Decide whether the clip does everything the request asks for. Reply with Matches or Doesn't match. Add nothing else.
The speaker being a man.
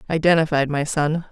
Doesn't match